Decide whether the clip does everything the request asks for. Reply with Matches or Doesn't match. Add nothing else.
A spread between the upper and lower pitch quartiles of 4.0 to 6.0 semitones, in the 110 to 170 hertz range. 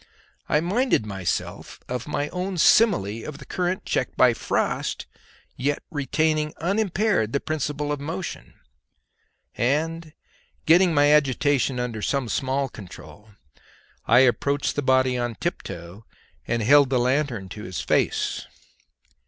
Matches